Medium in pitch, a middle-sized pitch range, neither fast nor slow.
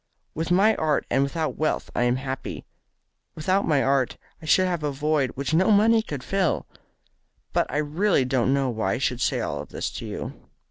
Yes: medium, 150 Hz; average, 5.0 semitones; average, 195 wpm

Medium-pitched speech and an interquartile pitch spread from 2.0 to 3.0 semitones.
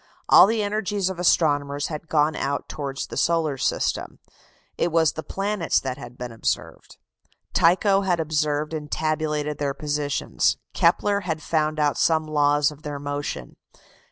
Yes: medium, 155 Hz; narrow, 2.5 semitones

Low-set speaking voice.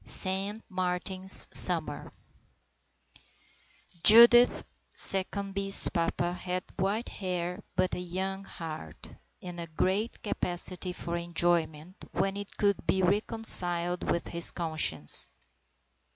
No: medium, 180 Hz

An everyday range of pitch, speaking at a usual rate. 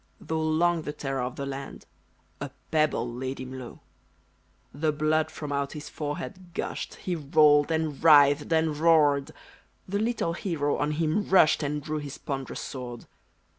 No: narrow, 2.3 semitones; average, 160 wpm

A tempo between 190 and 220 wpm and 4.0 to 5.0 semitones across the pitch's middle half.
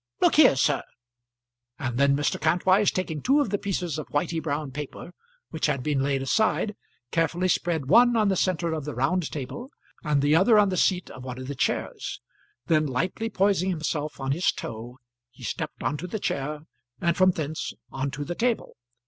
Yes: average, 195 wpm; average, 4.7 semitones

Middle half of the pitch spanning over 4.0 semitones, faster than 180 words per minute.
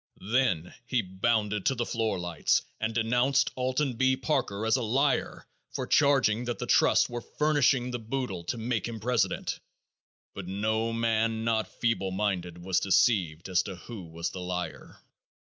No: average, 4.5 semitones; average, 160 wpm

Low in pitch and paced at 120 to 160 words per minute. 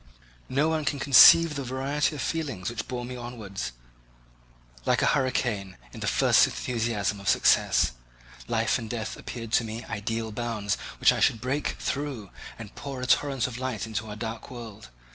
No: low, 120 Hz; average, 180 wpm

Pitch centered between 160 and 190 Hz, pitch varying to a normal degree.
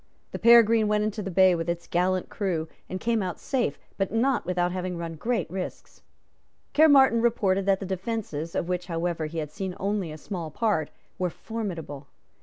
Yes: medium, 185 Hz; average, 4.2 semitones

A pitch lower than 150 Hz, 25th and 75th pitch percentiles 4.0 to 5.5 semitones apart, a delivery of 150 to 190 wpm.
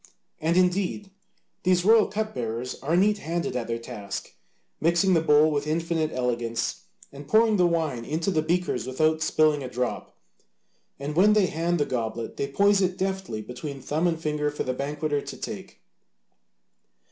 No: medium, 155 Hz; average, 5.2 semitones; average, 170 wpm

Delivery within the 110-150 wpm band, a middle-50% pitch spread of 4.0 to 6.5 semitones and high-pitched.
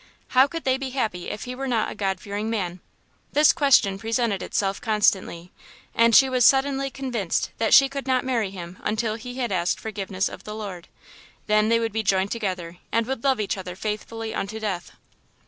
No: average, 200 wpm; average, 4.5 semitones; high, 220 Hz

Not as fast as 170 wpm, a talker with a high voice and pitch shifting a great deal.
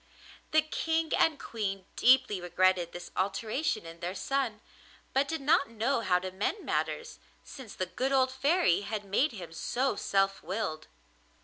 Yes: average, 155 wpm; high, 215 Hz; wide, 6.5 semitones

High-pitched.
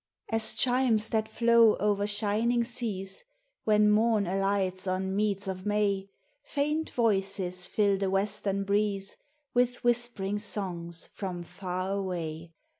Yes: high, 205 Hz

